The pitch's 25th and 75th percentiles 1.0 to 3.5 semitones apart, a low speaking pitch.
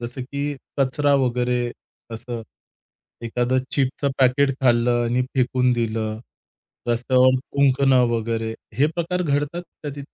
Yes: average, 2.7 semitones; low, 125 Hz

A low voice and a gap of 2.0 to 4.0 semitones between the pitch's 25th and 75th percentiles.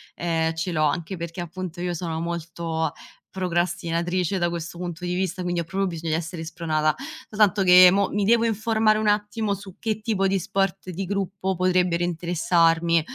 No: medium, 175 Hz; narrow, 2.5 semitones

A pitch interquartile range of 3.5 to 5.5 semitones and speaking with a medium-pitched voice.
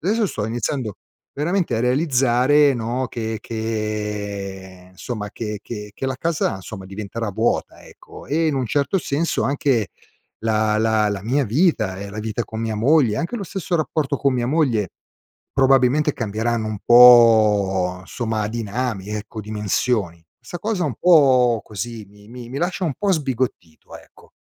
No: average, 4.7 semitones; low, 115 Hz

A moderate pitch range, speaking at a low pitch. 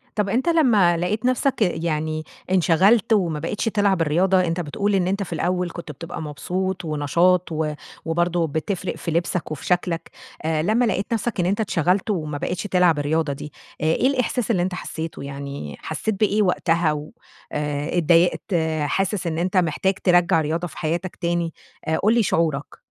No: average, 3.5 semitones; medium, 175 Hz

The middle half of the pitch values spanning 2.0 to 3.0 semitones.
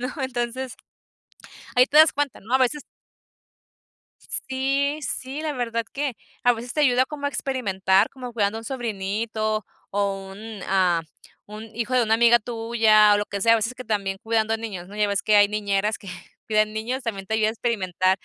No: average, 3.5 semitones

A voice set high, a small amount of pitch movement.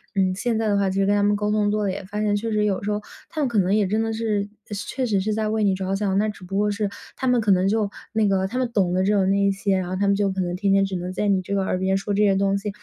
Yes: high, 200 Hz; narrow, 1.6 semitones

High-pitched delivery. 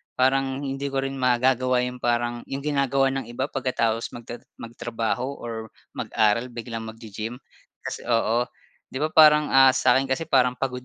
No: low, 125 Hz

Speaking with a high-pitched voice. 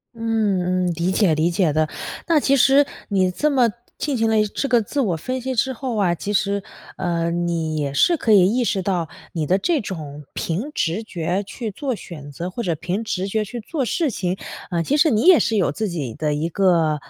Yes: high, 195 Hz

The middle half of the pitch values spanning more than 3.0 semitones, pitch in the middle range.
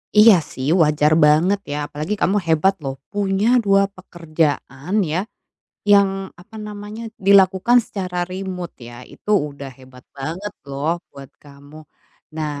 Yes: average, 5.2 semitones; medium, 180 Hz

